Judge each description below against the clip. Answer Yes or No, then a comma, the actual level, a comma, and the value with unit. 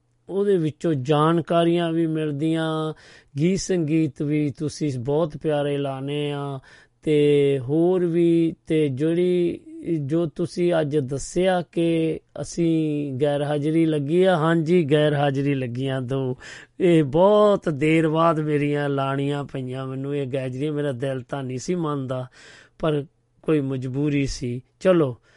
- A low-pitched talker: No, medium, 150 Hz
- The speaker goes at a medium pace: Yes, average, 130 wpm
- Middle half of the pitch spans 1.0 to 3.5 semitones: Yes, average, 3.0 semitones